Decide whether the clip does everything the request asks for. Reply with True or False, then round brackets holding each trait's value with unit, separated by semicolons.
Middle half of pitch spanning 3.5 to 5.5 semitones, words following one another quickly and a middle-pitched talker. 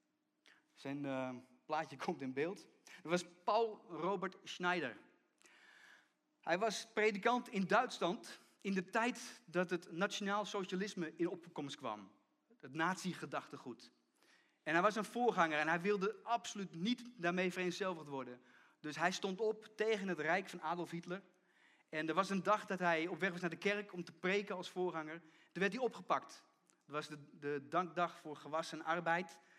False (3.8 semitones; 165 wpm; 180 Hz)